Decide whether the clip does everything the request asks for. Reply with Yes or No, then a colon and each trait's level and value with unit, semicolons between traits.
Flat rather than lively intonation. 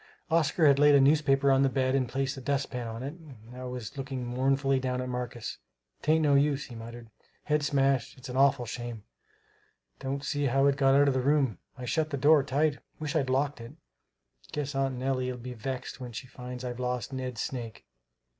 Yes: narrow, 2.0 semitones